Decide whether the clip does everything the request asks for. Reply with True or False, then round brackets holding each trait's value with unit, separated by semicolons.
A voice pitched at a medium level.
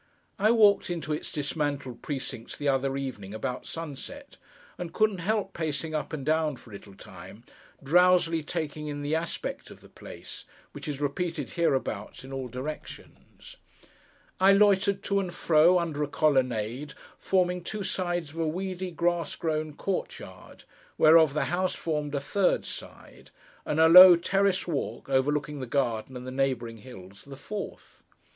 True (155 Hz)